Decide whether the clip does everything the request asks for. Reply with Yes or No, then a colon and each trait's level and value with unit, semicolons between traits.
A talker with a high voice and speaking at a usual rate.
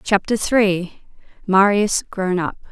No: high, 195 Hz; slow, 90 wpm